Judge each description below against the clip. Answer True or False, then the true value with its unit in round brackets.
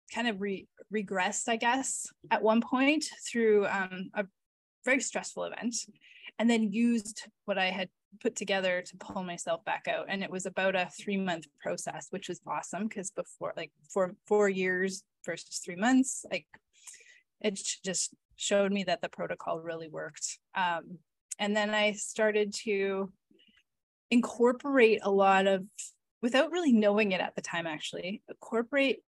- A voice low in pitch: False (205 Hz)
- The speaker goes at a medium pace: True (155 wpm)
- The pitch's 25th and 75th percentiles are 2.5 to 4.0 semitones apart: True (3.6 semitones)